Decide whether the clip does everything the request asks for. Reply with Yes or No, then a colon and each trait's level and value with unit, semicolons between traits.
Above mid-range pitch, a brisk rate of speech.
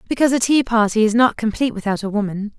Yes: high, 225 Hz; fast, 230 wpm